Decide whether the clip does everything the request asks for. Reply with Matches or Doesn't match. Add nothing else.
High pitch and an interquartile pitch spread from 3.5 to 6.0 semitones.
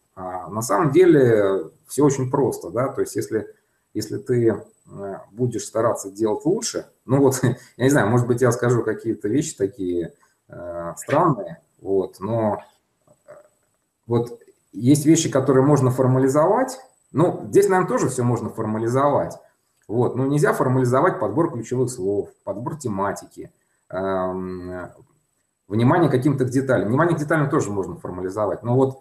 Doesn't match